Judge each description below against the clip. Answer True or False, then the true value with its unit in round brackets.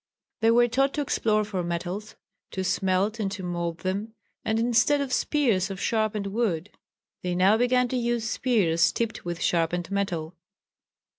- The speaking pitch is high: True (205 Hz)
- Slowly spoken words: False (160 wpm)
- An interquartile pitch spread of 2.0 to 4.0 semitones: False (4.5 semitones)